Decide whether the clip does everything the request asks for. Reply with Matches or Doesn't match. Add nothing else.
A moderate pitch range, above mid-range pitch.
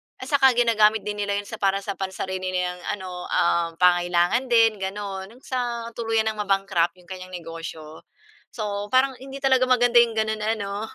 Matches